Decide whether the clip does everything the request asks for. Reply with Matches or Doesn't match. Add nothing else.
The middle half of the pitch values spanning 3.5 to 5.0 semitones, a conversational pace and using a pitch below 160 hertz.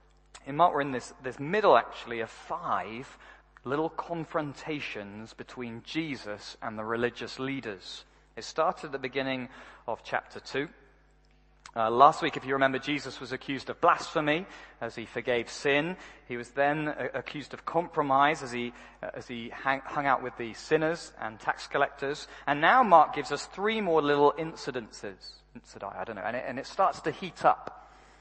Matches